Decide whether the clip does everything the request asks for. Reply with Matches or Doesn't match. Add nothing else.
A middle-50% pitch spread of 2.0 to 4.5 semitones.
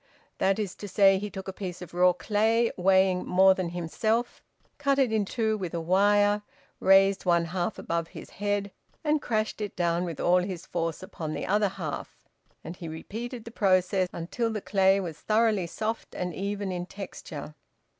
Matches